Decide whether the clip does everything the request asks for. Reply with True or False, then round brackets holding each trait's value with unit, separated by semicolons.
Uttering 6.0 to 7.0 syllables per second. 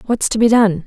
False (5.6 syllables/s)